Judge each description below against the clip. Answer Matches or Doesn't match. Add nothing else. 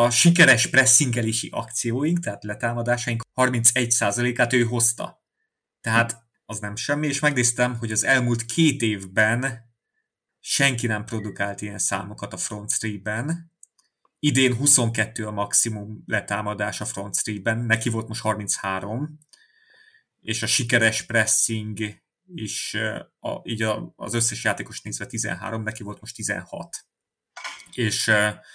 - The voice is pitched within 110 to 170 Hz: Matches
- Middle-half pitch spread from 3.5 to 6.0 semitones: Doesn't match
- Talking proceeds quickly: Doesn't match